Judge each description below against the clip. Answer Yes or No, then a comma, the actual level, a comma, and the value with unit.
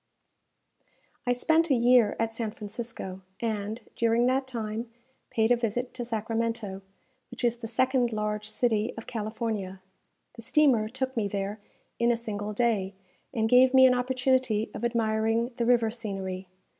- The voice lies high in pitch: Yes, high, 230 Hz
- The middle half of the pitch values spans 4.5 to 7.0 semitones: No, narrow, 2.4 semitones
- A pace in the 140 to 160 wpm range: Yes, average, 155 wpm